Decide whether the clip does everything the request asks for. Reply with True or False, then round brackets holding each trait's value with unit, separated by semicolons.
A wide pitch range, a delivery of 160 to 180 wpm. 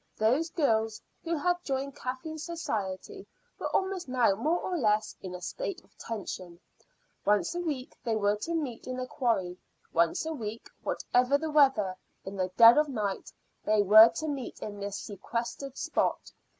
True (6.6 semitones; 170 wpm)